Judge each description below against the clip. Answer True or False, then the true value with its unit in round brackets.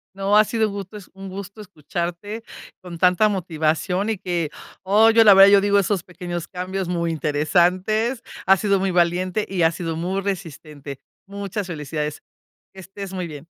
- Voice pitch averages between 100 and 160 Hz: False (185 Hz)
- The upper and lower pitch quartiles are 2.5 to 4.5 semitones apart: True (2.8 semitones)